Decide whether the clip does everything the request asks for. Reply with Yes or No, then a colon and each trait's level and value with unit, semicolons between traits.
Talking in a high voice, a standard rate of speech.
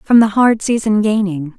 Yes: high, 210 Hz; average, 190 wpm